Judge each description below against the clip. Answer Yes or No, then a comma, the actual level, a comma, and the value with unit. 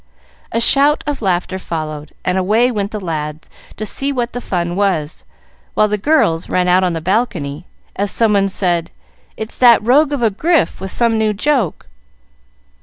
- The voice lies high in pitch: Yes, high, 200 Hz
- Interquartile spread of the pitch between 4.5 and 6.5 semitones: Yes, average, 5.2 semitones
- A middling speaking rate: Yes, average, 175 wpm